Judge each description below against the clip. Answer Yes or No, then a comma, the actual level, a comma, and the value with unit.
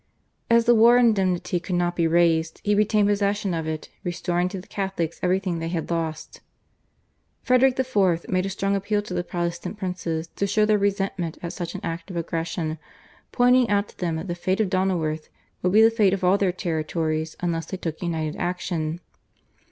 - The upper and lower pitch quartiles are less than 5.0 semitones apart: Yes, average, 3.3 semitones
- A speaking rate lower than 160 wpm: No, average, 190 wpm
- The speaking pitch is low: No, medium, 180 Hz